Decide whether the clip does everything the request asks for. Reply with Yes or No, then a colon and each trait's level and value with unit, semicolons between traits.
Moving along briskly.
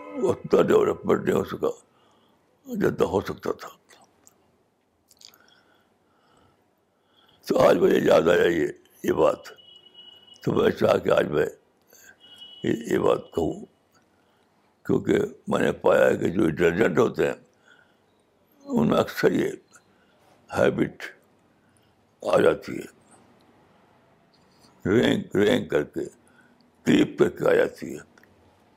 No: slow, 110 wpm